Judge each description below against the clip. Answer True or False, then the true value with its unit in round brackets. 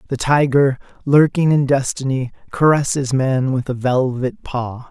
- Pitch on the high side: False (135 Hz)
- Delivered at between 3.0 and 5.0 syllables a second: True (4.5 syllables/s)